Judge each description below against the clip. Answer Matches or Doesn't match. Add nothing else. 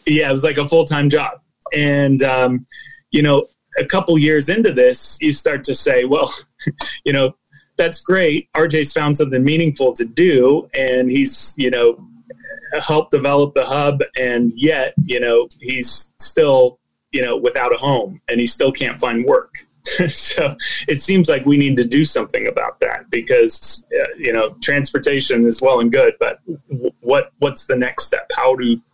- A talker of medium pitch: Matches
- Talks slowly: Doesn't match